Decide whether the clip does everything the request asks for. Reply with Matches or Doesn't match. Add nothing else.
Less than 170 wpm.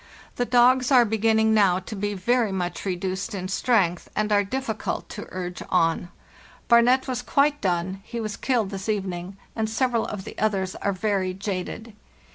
Doesn't match